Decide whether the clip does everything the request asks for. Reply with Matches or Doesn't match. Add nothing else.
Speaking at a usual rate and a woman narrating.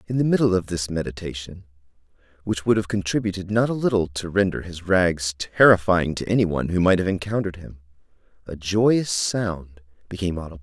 Doesn't match